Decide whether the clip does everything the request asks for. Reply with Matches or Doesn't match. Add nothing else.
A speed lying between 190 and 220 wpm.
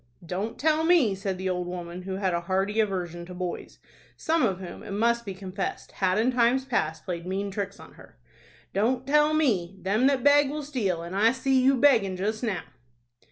Matches